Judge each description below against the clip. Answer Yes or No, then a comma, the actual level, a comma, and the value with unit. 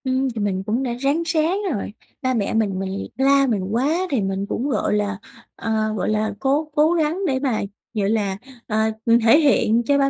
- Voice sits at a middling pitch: No, high, 235 Hz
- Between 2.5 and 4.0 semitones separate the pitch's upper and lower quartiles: No, average, 4.9 semitones